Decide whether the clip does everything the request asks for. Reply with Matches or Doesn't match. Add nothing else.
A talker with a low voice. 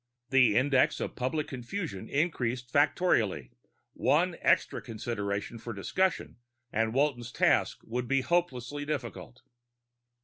Matches